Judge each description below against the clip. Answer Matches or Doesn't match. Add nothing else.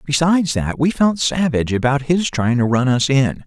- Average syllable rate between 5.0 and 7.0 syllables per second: Matches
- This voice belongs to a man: Matches